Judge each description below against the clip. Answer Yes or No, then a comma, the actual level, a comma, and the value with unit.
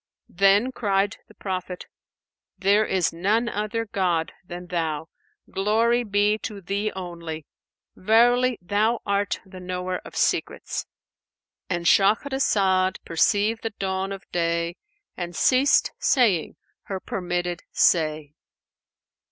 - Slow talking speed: Yes, slow, 110 wpm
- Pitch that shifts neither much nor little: Yes, average, 3.3 semitones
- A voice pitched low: No, high, 195 Hz